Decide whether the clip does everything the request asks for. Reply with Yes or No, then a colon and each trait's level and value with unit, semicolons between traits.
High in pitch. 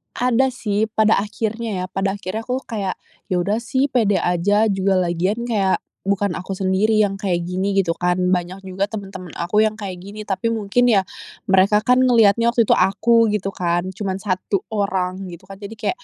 Yes: high, 200 Hz